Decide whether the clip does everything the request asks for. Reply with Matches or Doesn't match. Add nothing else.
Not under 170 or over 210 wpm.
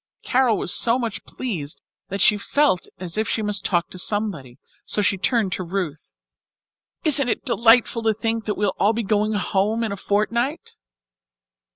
Matches